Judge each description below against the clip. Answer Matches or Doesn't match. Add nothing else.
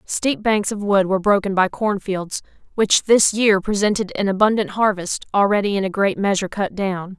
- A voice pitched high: Matches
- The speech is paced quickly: Doesn't match